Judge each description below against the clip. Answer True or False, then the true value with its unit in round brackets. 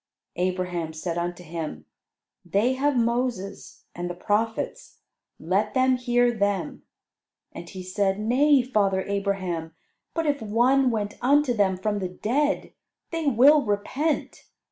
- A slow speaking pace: True (130 wpm)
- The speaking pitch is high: True (210 Hz)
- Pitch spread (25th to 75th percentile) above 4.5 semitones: True (5.6 semitones)